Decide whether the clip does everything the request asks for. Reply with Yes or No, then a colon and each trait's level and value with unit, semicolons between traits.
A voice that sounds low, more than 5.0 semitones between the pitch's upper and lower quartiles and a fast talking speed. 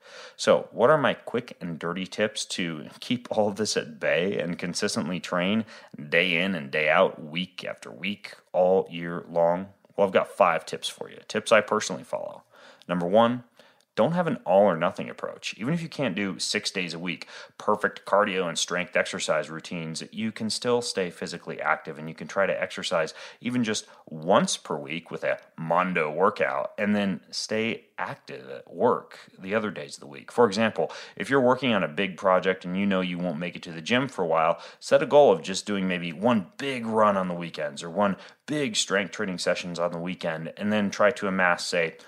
Yes: very low, 95 Hz; wide, 5.6 semitones; fast, 210 wpm